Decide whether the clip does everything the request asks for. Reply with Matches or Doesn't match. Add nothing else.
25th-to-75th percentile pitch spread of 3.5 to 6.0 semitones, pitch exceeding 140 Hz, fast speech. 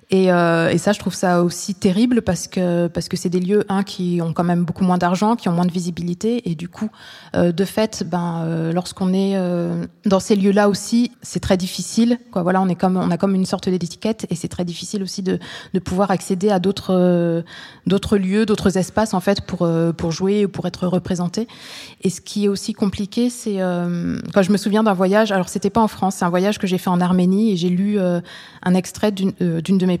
Doesn't match